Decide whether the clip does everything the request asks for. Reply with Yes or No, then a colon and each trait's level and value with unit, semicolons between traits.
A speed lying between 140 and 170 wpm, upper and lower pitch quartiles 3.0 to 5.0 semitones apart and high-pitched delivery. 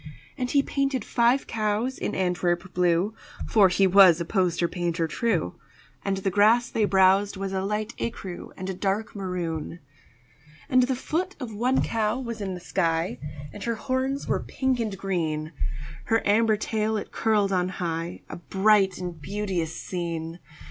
Yes: average, 165 wpm; average, 4.0 semitones; high, 195 Hz